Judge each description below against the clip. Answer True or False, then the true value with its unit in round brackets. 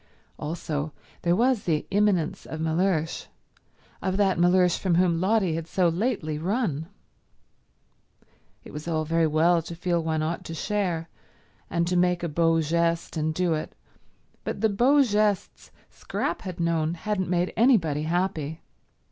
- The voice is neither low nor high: True (170 Hz)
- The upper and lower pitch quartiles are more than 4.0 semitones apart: False (2.9 semitones)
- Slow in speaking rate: False (150 wpm)